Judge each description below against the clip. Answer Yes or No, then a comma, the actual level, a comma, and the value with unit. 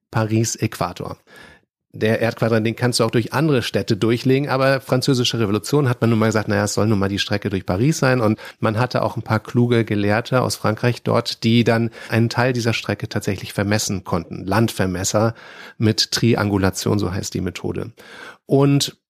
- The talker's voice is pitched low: Yes, low, 115 Hz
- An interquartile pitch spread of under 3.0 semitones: Yes, narrow, 2.5 semitones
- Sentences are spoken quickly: No, average, 180 wpm